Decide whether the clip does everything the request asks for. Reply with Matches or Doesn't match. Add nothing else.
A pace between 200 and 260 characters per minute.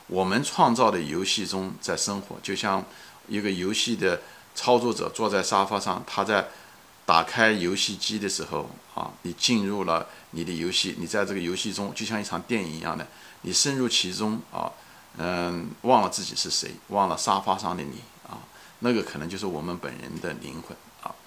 Doesn't match